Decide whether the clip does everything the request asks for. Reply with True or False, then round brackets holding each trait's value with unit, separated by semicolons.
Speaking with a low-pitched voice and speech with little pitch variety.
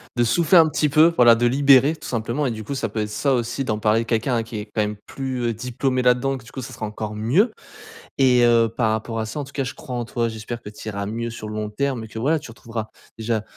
False (120 Hz; 3.3 semitones)